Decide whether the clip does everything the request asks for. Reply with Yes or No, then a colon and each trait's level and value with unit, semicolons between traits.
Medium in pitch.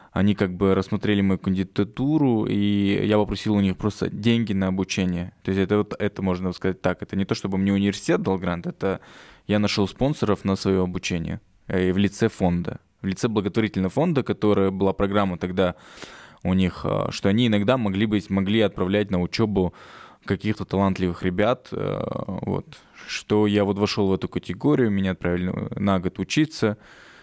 No: low, 100 Hz